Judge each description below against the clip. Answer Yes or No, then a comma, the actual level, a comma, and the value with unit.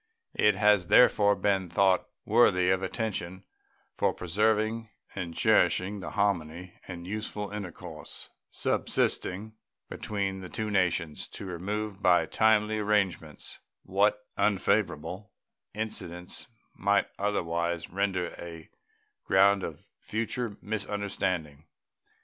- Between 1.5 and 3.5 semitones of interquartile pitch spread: Yes, average, 2.8 semitones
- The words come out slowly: Yes, slow, 105 wpm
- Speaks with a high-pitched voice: No, low, 100 Hz